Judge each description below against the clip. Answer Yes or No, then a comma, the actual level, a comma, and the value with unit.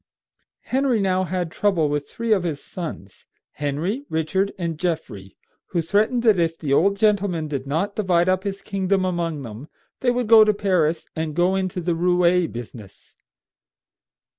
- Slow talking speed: No, average, 165 wpm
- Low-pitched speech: No, medium, 180 Hz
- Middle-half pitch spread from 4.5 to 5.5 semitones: No, average, 3.9 semitones